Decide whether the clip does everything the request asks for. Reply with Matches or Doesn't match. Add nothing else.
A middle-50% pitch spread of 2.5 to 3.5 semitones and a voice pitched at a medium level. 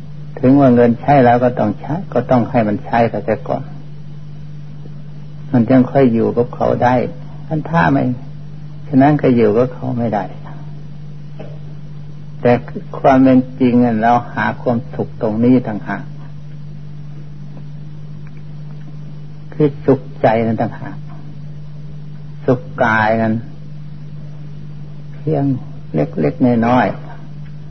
Matches